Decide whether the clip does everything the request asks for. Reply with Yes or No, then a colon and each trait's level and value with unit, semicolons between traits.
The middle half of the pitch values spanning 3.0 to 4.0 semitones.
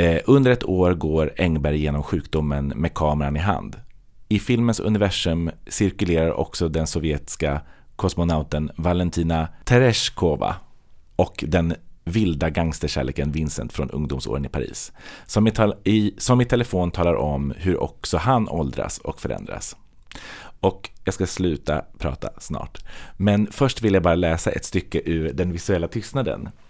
No: average, 4.7 semitones